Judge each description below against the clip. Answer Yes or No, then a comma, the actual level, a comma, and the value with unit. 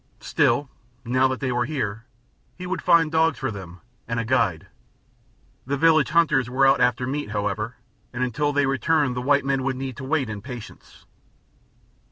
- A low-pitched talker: Yes, low, 130 Hz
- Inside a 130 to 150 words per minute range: No, average, 180 wpm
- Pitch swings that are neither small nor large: Yes, average, 3.3 semitones